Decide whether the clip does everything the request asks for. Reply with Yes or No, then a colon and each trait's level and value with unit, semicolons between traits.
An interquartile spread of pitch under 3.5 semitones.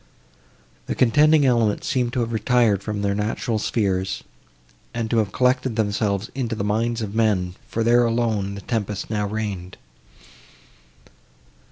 Yes: narrow, 2.6 semitones